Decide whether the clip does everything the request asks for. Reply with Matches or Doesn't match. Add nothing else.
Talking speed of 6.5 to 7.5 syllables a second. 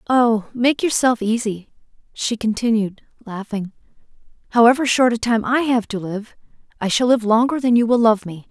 Doesn't match